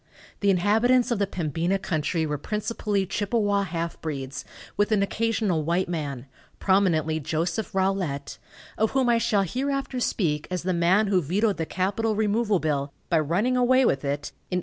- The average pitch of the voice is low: No, high, 190 Hz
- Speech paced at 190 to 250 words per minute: No, average, 170 wpm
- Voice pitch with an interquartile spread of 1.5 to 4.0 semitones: No, average, 5.1 semitones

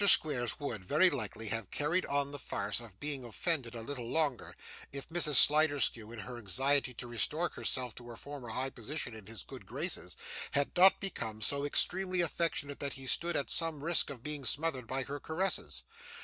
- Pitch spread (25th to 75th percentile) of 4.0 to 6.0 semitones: Yes, average, 4.4 semitones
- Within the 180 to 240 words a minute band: Yes, average, 190 wpm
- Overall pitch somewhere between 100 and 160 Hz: Yes, medium, 140 Hz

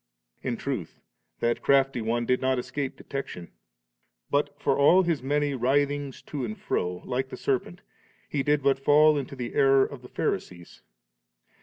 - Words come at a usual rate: Yes, average, 160 wpm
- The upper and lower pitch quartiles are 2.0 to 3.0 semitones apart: Yes, narrow, 2.5 semitones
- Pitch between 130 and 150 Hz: Yes, low, 135 Hz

